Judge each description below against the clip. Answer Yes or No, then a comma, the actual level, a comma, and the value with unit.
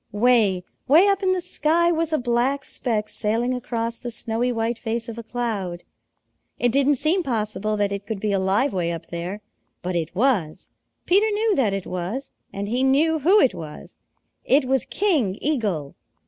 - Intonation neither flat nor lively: No, wide, 5.7 semitones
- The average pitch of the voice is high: Yes, high, 235 Hz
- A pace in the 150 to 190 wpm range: Yes, average, 180 wpm